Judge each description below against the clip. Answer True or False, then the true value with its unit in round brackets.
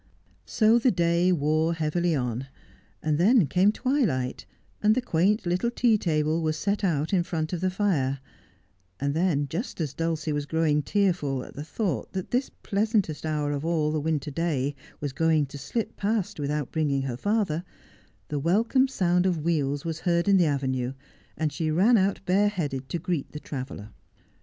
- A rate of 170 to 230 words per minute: True (175 wpm)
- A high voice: False (165 Hz)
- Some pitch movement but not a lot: True (4.6 semitones)